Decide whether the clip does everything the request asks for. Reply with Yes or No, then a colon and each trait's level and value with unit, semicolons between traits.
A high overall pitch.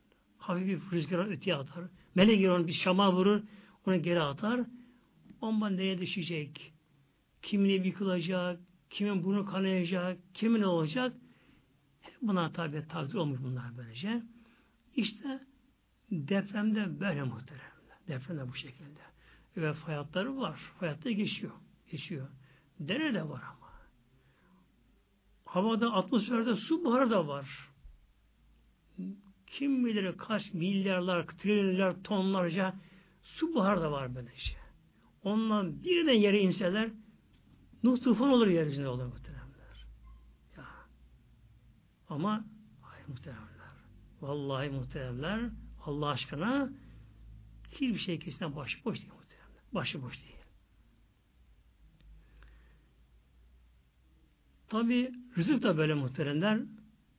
No: medium, 180 Hz